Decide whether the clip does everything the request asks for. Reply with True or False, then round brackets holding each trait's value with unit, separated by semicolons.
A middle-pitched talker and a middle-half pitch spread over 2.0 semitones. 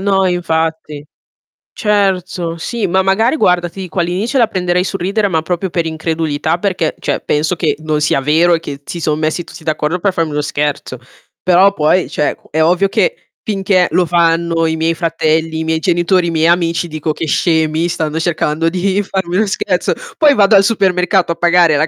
True (170 Hz; 2.9 semitones)